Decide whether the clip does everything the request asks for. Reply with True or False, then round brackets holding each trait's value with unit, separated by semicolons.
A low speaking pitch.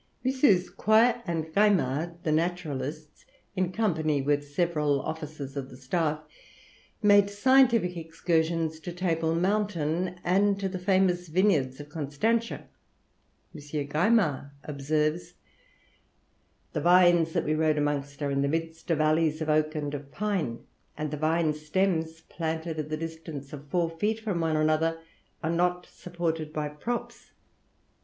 False (160 Hz)